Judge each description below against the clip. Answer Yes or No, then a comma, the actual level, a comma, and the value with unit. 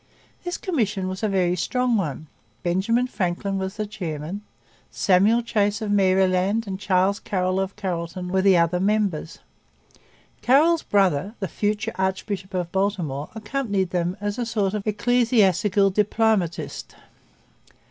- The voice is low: No, high, 195 Hz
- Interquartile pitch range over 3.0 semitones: No, narrow, 2.6 semitones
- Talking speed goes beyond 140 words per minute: No, slow, 135 wpm